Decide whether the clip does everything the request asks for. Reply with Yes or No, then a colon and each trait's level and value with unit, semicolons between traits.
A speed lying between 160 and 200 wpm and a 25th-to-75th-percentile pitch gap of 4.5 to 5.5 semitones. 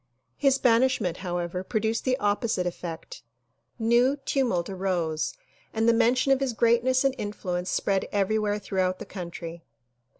No: average, 140 wpm; average, 5.1 semitones